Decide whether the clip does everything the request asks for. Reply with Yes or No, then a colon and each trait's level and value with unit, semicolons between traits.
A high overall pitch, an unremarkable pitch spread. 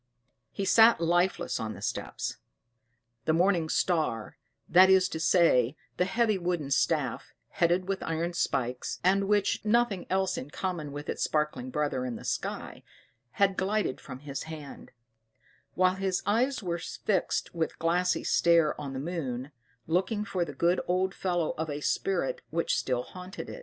No: medium, 175 Hz; average, 4.1 semitones